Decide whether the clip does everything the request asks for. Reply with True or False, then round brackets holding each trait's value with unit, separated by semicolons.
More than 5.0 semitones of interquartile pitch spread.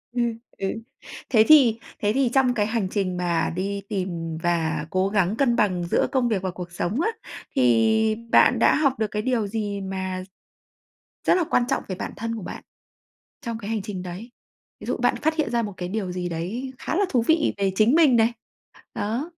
False (4.5 semitones)